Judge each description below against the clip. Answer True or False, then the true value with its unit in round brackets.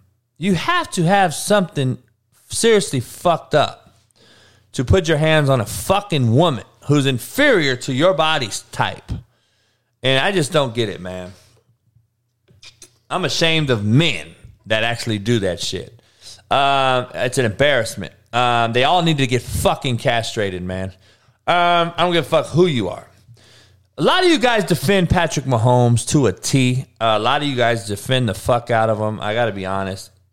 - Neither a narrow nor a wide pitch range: True (4.9 semitones)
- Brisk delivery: False (170 wpm)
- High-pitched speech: False (120 Hz)